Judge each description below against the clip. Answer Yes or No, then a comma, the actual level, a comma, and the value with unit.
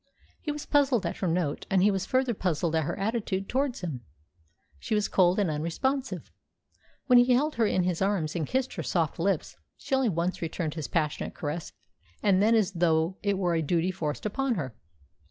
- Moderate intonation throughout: No, wide, 5.8 semitones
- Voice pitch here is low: No, medium, 185 Hz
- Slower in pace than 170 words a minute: No, average, 200 wpm